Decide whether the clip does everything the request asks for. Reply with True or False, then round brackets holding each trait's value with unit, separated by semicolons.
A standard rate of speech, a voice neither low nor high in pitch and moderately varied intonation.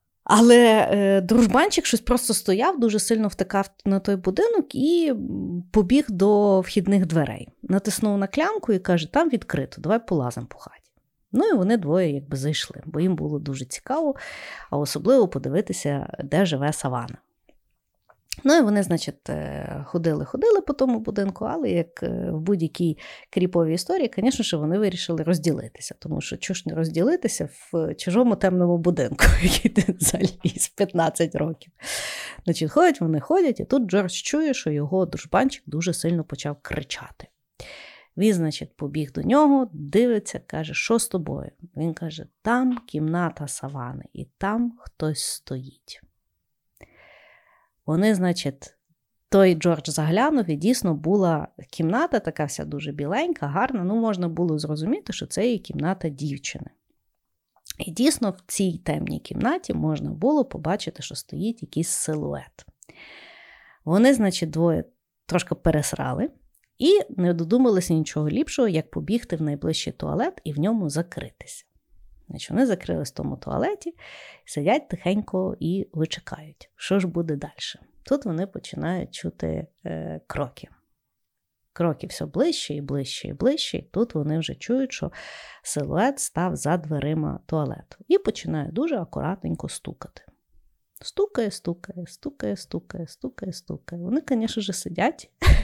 False (135 wpm; 180 Hz; 6.1 semitones)